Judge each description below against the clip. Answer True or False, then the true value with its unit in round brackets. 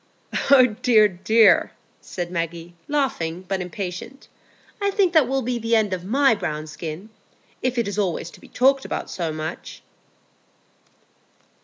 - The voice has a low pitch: False (205 Hz)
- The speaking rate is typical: True (150 wpm)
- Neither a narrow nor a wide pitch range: False (6.5 semitones)